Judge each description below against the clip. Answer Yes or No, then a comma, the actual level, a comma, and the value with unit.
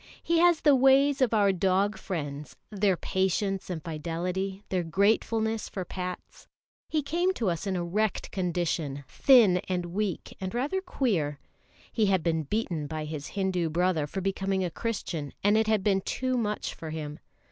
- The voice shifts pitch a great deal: No, average, 4.4 semitones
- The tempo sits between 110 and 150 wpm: No, average, 170 wpm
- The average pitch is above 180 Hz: Yes, high, 190 Hz